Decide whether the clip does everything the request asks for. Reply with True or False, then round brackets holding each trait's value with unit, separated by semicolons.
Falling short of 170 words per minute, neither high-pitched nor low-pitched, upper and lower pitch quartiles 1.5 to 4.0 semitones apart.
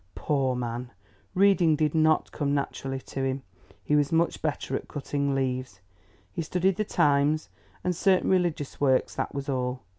True (160 wpm; 145 Hz; 3.4 semitones)